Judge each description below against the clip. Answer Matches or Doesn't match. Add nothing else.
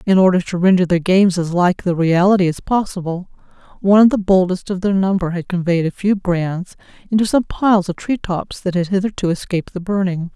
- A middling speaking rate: Doesn't match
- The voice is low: Doesn't match